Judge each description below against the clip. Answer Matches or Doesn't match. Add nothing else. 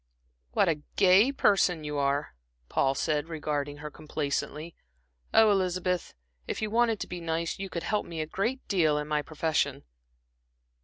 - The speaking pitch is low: Doesn't match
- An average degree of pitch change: Matches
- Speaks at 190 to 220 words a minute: Doesn't match